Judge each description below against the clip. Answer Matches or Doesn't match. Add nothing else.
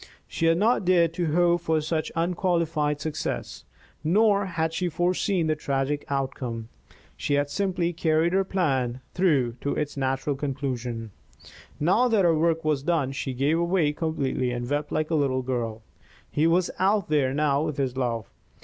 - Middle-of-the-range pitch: Matches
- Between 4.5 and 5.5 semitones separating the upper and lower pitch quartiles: Doesn't match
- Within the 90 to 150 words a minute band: Doesn't match